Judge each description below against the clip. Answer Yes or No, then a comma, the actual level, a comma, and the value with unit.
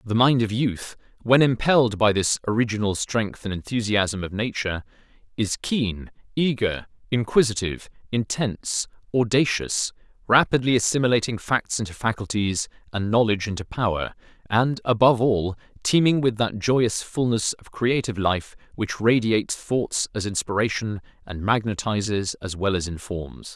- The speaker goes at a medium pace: No, slow, 130 wpm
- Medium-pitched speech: No, low, 110 Hz